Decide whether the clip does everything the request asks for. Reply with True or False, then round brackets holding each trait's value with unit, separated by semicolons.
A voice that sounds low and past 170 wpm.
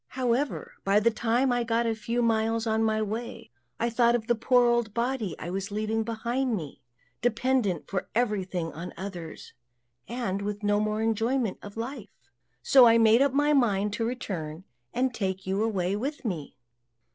False (225 Hz; 180 wpm)